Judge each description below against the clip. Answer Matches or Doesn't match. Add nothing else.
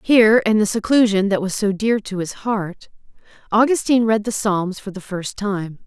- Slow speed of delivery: Doesn't match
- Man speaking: Doesn't match